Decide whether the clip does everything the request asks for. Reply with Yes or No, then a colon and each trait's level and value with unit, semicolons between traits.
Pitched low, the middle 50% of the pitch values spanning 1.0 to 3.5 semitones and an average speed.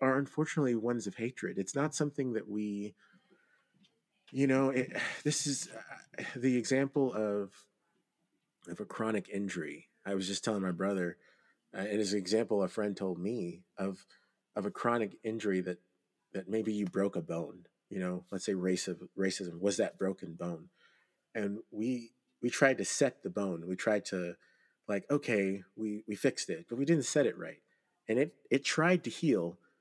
No: low, 105 Hz; average, 4.2 semitones; average, 180 wpm